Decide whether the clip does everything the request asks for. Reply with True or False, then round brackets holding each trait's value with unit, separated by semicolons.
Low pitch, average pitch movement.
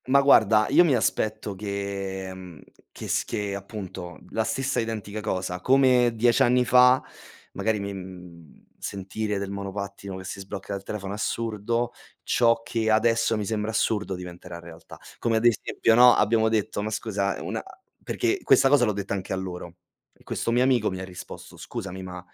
True (105 Hz; 3.4 semitones)